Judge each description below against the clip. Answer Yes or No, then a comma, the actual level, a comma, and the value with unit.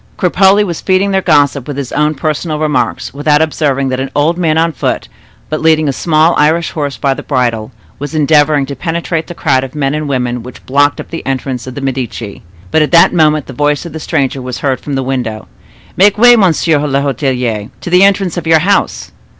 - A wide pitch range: No, average, 3.4 semitones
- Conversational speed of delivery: No, fast, 215 wpm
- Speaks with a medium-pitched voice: Yes, medium, 150 Hz